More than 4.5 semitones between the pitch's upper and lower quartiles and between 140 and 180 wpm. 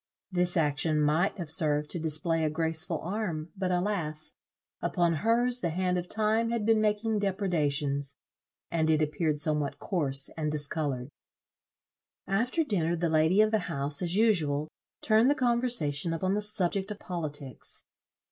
Yes: average, 5.2 semitones; average, 150 wpm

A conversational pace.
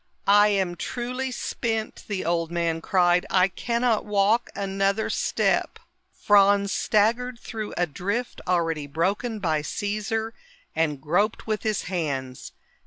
No: slow, 125 wpm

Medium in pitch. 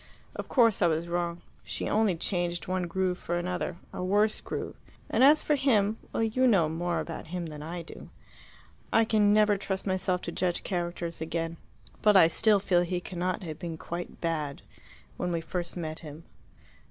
Yes: medium, 175 Hz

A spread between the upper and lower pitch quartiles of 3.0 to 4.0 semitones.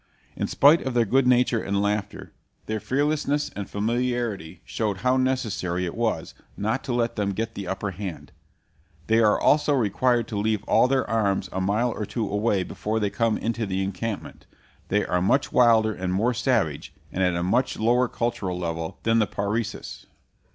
Yes: average, 3.7 semitones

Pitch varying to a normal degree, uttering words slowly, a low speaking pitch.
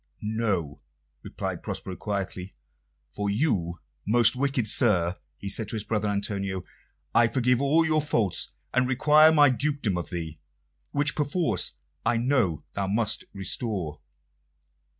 No: wide, 5.8 semitones; slow, 130 wpm; low, 110 Hz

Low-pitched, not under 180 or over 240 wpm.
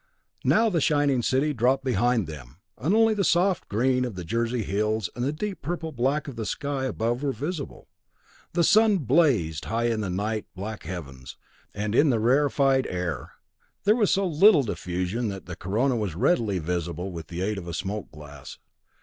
Yes: low, 120 Hz; average, 185 wpm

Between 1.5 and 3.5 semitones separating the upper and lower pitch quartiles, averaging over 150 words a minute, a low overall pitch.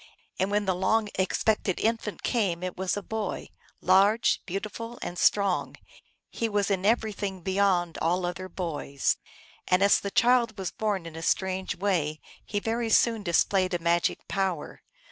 No: average, 2.8 semitones; average, 160 wpm; high, 195 Hz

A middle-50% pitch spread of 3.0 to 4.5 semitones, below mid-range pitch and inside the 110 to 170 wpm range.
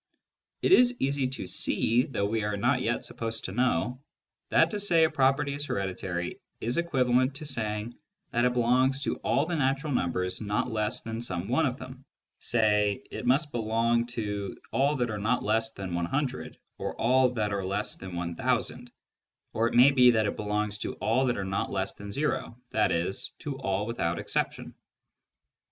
No: average, 4.2 semitones; low, 120 Hz; average, 180 wpm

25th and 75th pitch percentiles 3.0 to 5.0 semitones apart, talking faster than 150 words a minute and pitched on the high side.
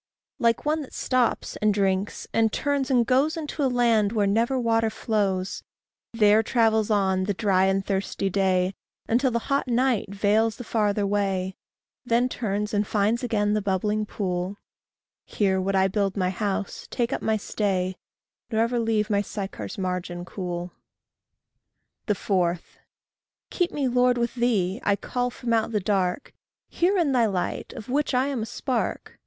Yes: average, 3.7 semitones; average, 165 wpm; high, 215 Hz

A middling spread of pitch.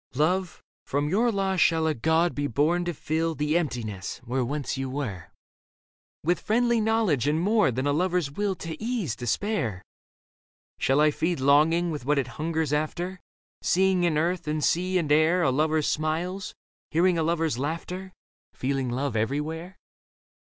Yes: average, 3.9 semitones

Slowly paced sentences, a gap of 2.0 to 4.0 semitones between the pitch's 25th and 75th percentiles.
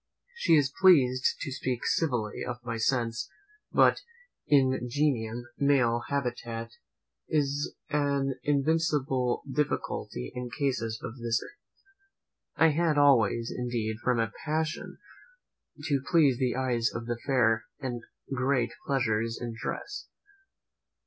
Yes: slow, 115 wpm; average, 3.4 semitones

